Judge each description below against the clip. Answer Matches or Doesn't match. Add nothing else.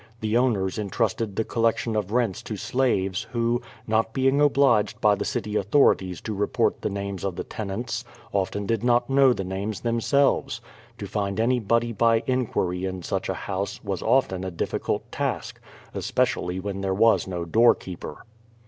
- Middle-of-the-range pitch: Doesn't match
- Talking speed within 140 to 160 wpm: Doesn't match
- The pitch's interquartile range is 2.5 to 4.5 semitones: Matches